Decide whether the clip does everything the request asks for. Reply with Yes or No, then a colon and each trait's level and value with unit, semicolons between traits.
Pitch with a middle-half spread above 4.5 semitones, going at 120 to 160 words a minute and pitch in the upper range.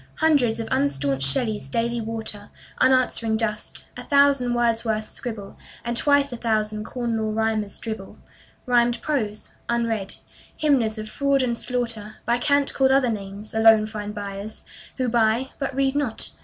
No: average, 2.9 semitones; average, 150 wpm; high, 230 Hz